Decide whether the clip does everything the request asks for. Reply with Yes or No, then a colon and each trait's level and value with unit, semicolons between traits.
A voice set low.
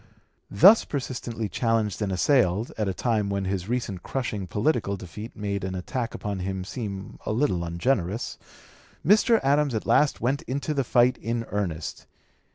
Yes: low, 110 Hz